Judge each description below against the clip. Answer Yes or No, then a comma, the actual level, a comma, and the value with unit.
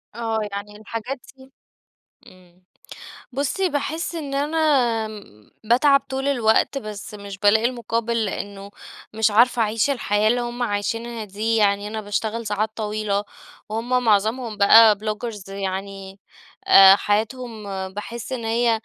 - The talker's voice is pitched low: No, high, 220 Hz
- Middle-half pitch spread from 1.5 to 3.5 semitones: Yes, average, 2.8 semitones